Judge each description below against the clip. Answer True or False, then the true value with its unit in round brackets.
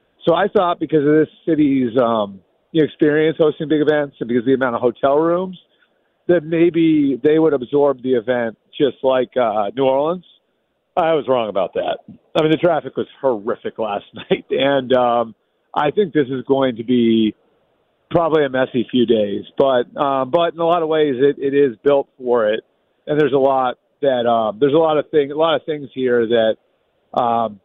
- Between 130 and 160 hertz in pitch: True (140 Hz)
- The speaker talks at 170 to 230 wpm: True (200 wpm)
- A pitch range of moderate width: True (4.1 semitones)